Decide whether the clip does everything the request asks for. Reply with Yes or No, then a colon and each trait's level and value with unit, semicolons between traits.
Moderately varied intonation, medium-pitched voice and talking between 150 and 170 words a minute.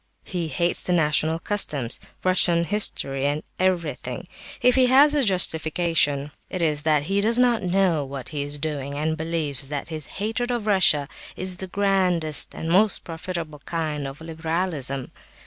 Yes: average, 4.2 semitones; medium, 165 Hz; average, 160 wpm